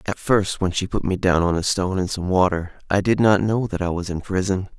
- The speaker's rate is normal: No, fast, 275 wpm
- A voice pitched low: Yes, very low, 95 Hz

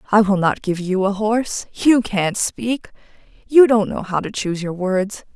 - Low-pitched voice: No, high, 205 Hz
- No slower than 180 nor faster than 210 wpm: Yes, average, 200 wpm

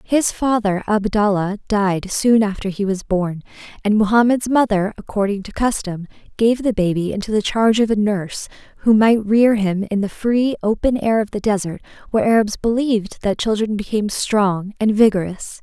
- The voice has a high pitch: Yes, high, 210 Hz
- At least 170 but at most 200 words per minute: Yes, average, 175 wpm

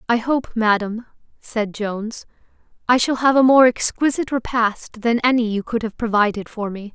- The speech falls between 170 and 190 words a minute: Yes, average, 175 wpm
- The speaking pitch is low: No, high, 230 Hz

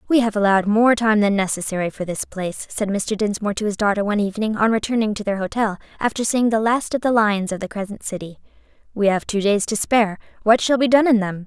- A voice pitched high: Yes, high, 210 Hz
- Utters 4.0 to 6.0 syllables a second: No, 6.4 syllables/s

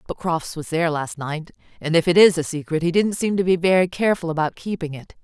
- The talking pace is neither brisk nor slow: No, fast, 250 wpm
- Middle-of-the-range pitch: Yes, medium, 170 Hz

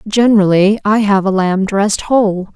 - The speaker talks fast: No, average, 165 wpm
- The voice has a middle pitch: No, high, 200 Hz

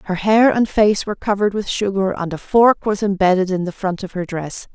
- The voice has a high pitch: Yes, high, 195 Hz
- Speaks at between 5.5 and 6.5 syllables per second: Yes, 5.6 syllables/s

